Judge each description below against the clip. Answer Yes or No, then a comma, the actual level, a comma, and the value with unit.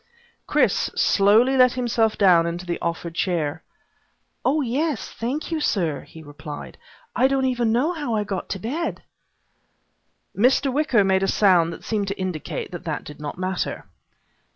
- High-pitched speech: Yes, high, 205 Hz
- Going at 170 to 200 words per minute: No, average, 160 wpm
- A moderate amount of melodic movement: No, wide, 6.7 semitones